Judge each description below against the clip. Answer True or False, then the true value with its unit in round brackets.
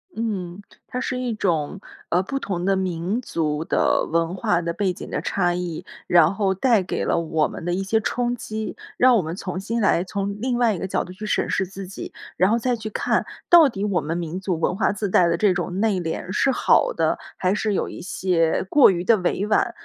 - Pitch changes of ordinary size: True (3.7 semitones)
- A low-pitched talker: False (190 Hz)